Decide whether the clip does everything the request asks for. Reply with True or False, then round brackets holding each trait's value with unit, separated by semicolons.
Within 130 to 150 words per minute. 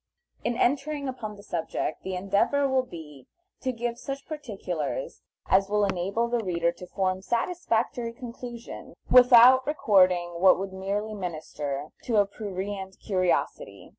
True (135 wpm)